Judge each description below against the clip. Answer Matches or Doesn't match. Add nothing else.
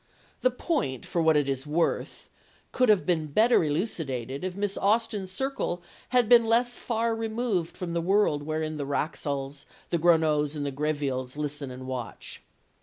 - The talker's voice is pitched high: Doesn't match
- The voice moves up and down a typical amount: Doesn't match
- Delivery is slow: Doesn't match